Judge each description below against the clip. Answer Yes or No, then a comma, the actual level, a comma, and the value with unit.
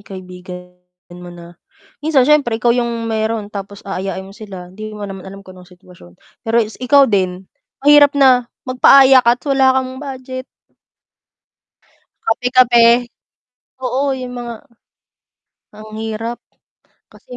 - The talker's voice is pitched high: Yes, high, 225 Hz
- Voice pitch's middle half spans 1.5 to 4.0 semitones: No, average, 4.8 semitones